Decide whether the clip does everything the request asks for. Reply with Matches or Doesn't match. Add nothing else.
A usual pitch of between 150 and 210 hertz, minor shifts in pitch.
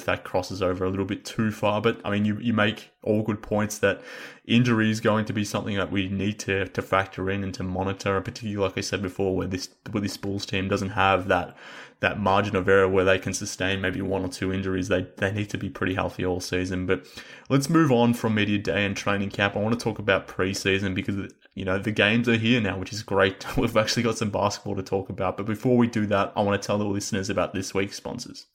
Doesn't match